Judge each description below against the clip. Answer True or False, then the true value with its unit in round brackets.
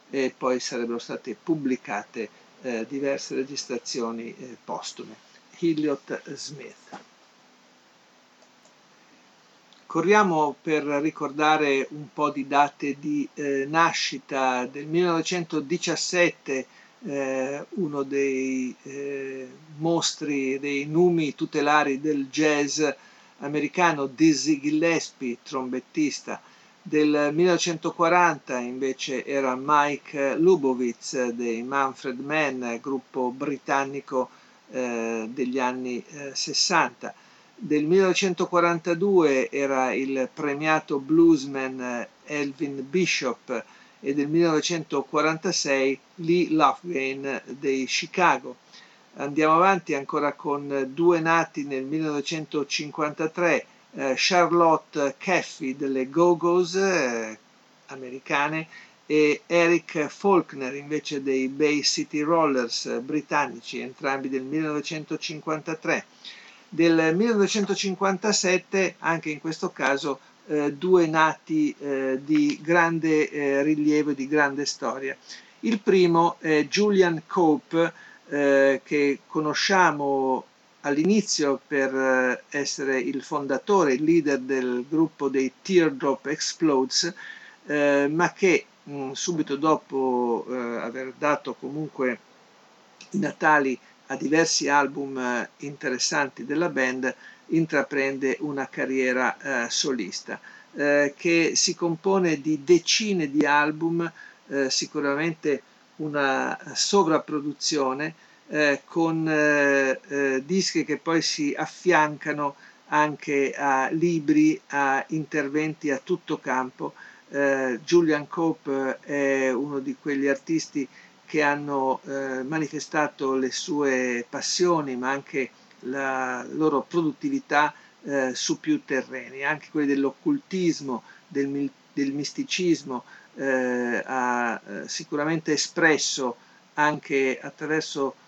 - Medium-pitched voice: True (145 Hz)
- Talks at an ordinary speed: False (95 wpm)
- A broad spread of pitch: False (3.3 semitones)